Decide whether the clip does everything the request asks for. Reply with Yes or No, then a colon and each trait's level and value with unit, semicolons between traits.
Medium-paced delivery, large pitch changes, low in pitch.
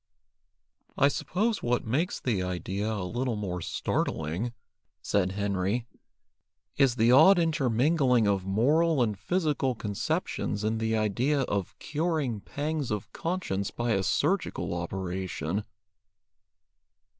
No: slow, 115 wpm; wide, 6.3 semitones; low, 115 Hz